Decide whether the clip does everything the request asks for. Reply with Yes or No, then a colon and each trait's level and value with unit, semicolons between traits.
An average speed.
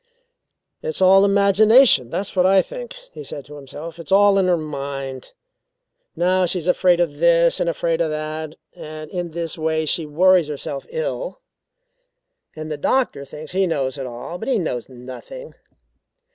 Yes: average, 165 wpm